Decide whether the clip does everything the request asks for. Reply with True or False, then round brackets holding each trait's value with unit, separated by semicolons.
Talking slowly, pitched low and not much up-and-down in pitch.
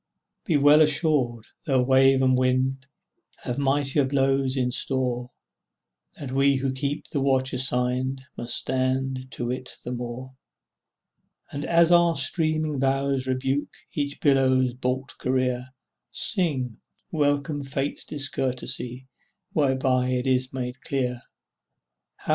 True (120 wpm; 130 Hz; 1.7 semitones)